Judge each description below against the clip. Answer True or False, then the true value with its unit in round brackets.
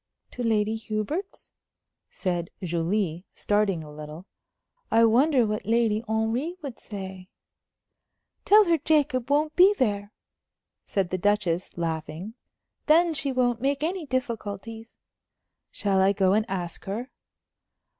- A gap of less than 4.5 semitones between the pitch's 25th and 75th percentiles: False (5.6 semitones)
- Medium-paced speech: False (125 wpm)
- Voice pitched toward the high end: True (220 Hz)